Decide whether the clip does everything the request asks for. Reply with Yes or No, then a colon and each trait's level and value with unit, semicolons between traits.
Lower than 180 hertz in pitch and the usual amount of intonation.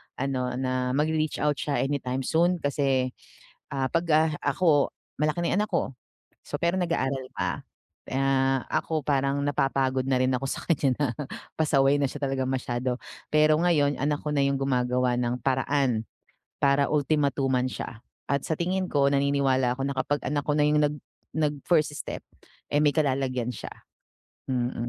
No: medium, 140 Hz; narrow, 2.3 semitones